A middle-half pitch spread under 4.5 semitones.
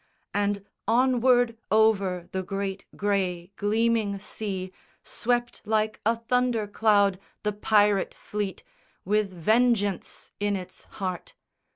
Yes: narrow, 2.4 semitones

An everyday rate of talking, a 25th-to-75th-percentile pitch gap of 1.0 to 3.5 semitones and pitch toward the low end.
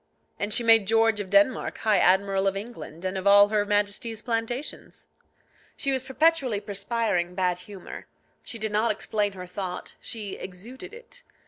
No: average, 160 wpm; average, 3.0 semitones; high, 210 Hz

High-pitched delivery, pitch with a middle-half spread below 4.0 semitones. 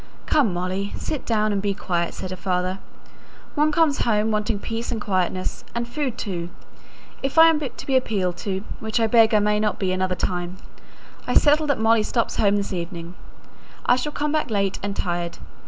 No: high, 210 Hz; average, 4.4 semitones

